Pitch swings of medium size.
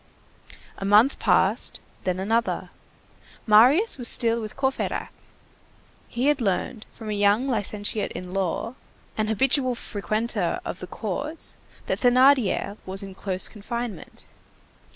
Yes: average, 3.8 semitones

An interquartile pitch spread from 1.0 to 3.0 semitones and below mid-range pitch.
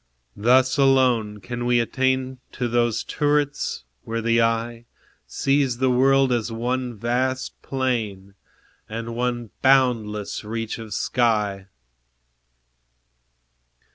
Yes: narrow, 2.5 semitones; low, 120 Hz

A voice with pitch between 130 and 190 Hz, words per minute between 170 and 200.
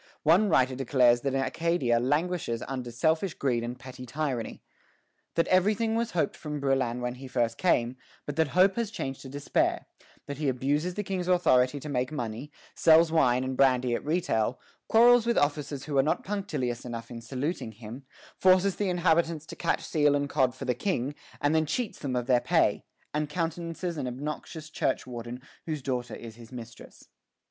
Yes: medium, 140 Hz; average, 180 wpm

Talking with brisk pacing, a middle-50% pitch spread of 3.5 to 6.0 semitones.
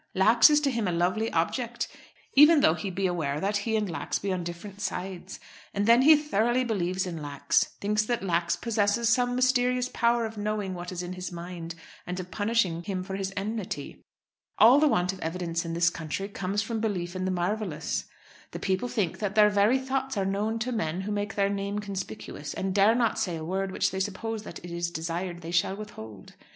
Yes: fast, 210 wpm; average, 4.0 semitones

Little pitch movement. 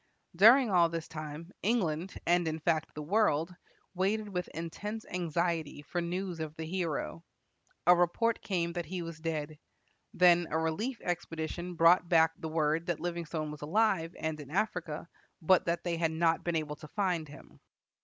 Yes: narrow, 2.1 semitones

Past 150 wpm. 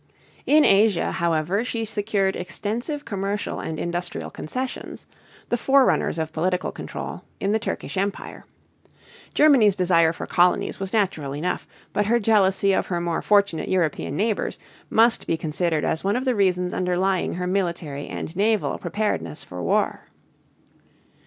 No: average, 145 wpm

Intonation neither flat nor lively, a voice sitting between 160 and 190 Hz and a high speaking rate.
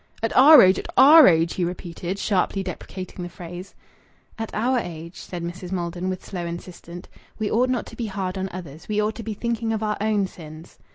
Yes: average, 3.8 semitones; medium, 185 Hz; fast, 210 wpm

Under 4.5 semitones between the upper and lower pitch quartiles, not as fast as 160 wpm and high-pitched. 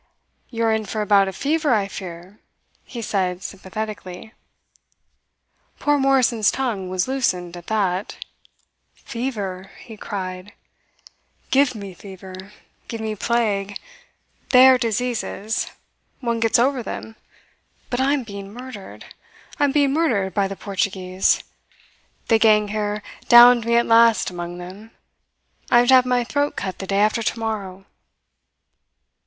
Yes: average, 3.9 semitones; average, 140 wpm; high, 215 Hz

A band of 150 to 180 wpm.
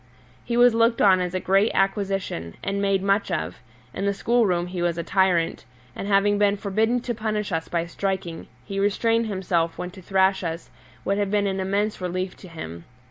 No: average, 200 wpm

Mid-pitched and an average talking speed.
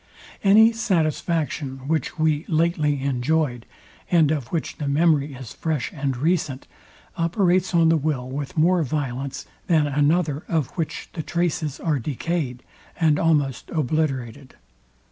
No: medium, 155 Hz; slow, 130 wpm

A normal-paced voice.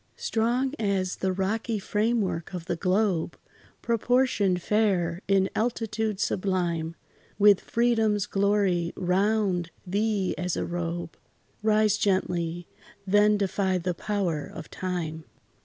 No: slow, 115 wpm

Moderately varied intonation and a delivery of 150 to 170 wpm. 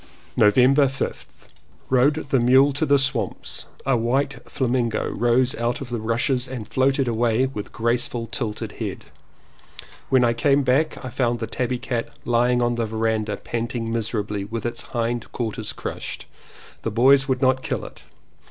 No: narrow, 2.3 semitones; average, 160 wpm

